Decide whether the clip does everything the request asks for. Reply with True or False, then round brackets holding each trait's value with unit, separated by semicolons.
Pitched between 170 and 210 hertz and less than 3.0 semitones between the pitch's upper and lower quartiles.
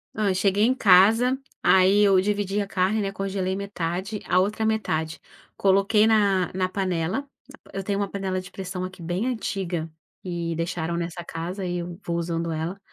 True (190 Hz; 2.5 semitones)